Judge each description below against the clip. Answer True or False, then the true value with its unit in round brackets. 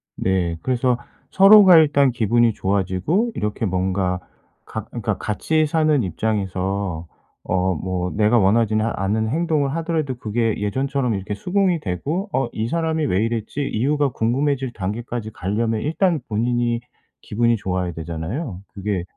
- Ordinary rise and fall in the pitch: False (6.6 semitones)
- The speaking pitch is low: True (115 Hz)